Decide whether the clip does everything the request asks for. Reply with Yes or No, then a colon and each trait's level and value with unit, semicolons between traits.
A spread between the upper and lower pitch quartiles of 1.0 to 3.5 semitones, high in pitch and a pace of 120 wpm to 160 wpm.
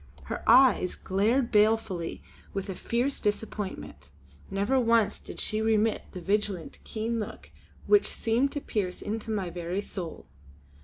Yes: average, 3.1 semitones; high, 215 Hz; average, 140 wpm